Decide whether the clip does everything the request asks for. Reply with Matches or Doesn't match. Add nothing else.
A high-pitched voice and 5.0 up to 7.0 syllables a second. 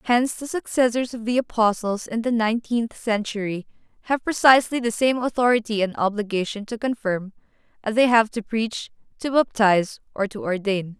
Matches